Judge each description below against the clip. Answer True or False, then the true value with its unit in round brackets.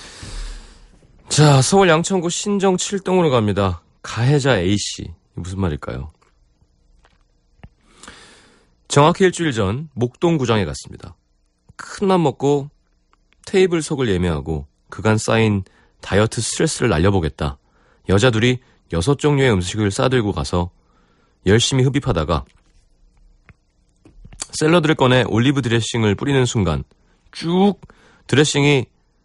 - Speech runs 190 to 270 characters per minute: True (245 characters per minute)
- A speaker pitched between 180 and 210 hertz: False (110 Hz)